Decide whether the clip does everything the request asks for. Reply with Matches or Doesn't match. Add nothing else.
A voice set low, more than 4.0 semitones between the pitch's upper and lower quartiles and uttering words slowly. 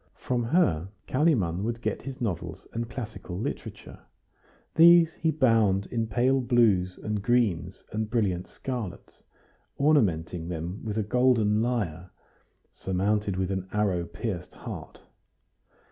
Matches